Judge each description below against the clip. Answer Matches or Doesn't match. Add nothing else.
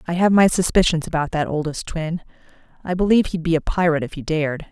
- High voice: Doesn't match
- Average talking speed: Doesn't match